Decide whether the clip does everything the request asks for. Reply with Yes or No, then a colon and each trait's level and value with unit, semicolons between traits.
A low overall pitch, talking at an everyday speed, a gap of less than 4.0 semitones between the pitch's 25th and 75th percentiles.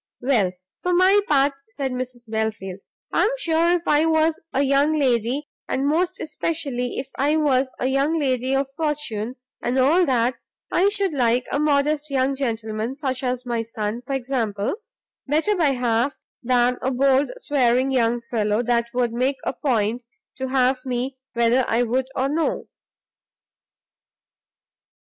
No: very high, 260 Hz; average, 155 wpm; average, 3.5 semitones